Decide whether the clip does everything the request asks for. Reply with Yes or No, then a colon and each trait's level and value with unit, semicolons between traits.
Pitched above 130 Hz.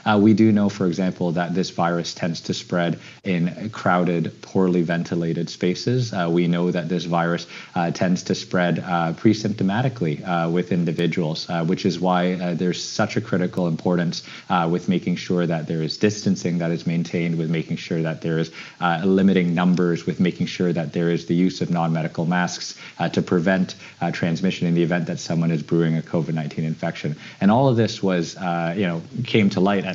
No: very low, 85 Hz